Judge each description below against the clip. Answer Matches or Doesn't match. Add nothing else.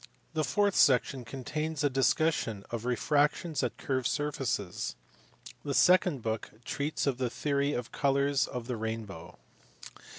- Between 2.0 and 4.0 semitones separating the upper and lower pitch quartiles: Matches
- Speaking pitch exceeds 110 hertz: Matches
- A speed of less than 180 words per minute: Matches